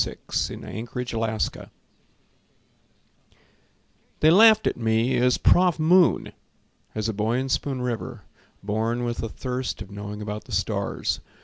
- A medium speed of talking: No, slow, 125 wpm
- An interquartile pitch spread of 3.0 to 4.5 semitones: Yes, average, 3.3 semitones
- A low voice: Yes, low, 120 Hz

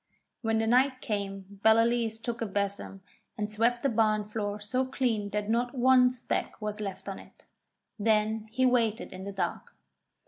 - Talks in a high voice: Yes, high, 220 Hz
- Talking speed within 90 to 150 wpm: No, average, 170 wpm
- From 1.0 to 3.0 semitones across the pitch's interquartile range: Yes, average, 2.7 semitones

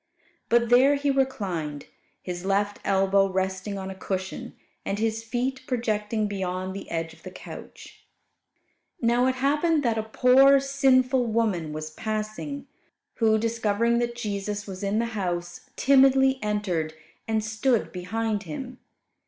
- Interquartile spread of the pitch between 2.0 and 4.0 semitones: No, average, 4.7 semitones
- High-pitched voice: Yes, high, 220 Hz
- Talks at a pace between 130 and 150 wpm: Yes, average, 140 wpm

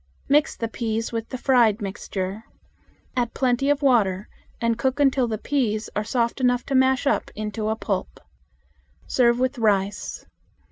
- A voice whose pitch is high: Yes, high, 235 Hz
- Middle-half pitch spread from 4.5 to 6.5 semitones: No, average, 3.4 semitones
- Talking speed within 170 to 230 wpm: No, average, 155 wpm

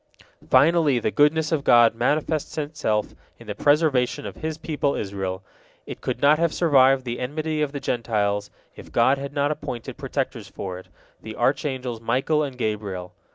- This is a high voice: No, low, 130 Hz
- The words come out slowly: No, average, 165 wpm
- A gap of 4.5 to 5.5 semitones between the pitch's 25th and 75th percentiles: Yes, average, 5.2 semitones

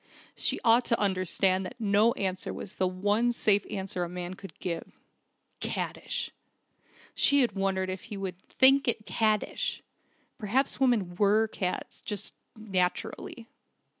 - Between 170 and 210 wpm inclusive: No, slow, 135 wpm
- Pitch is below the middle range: No, high, 200 Hz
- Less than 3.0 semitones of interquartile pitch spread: No, average, 3.3 semitones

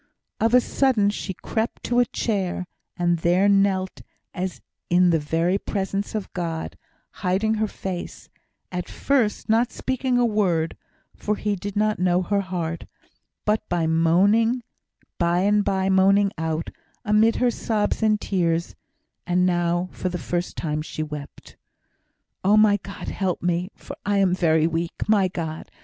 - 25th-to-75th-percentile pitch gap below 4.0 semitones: Yes, average, 3.4 semitones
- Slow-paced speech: No, average, 150 wpm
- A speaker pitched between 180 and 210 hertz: Yes, high, 190 Hz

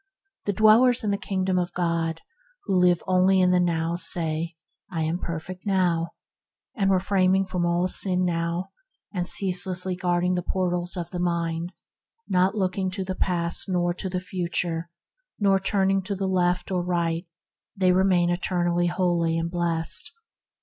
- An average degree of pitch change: No, narrow, 1.6 semitones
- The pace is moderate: Yes, average, 155 wpm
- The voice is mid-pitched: Yes, medium, 180 Hz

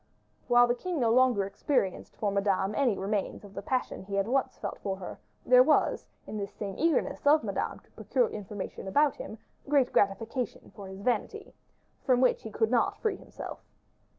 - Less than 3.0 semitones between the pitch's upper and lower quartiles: No, average, 5.0 semitones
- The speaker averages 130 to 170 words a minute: No, average, 185 wpm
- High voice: Yes, high, 225 Hz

